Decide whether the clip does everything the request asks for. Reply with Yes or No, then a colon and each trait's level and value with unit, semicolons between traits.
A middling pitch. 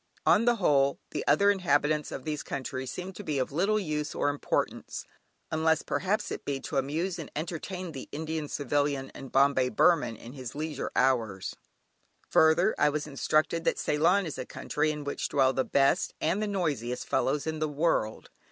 Yes: medium, 150 Hz